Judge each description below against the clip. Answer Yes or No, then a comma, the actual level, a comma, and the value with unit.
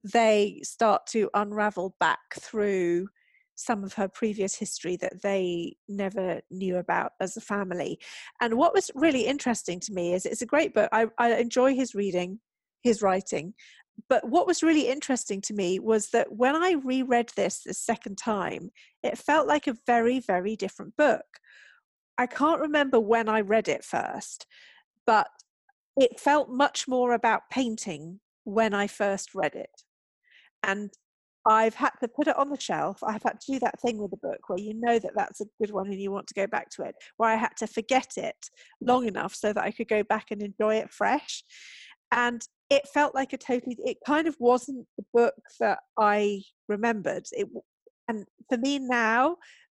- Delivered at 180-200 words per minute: Yes, average, 185 wpm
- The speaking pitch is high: Yes, high, 225 Hz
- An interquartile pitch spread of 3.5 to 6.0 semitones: Yes, average, 4.3 semitones